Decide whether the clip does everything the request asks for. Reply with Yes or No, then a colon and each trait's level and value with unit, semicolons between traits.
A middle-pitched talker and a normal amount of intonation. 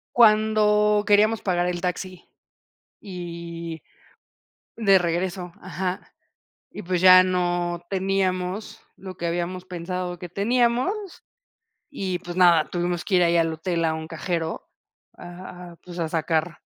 No: medium, 180 Hz; narrow, 2.1 semitones